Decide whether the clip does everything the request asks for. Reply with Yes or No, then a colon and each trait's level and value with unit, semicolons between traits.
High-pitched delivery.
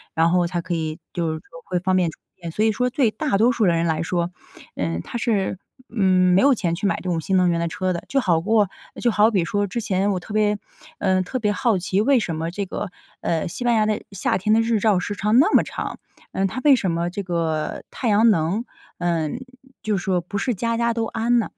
Yes: high, 195 Hz